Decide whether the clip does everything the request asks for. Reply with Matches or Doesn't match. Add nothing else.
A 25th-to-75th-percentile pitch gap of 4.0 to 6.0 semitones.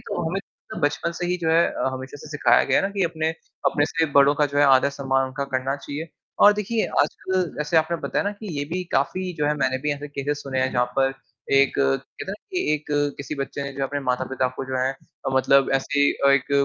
Doesn't match